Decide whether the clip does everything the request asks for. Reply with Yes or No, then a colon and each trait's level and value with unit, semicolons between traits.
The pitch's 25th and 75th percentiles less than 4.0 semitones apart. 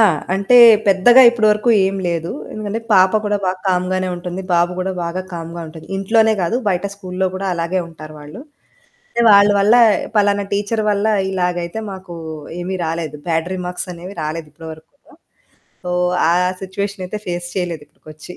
Yes: average, 2.8 semitones